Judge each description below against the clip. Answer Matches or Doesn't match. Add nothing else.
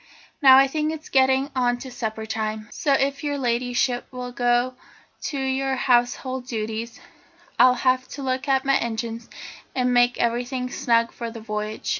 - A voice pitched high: Matches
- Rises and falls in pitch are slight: Matches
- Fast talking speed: Doesn't match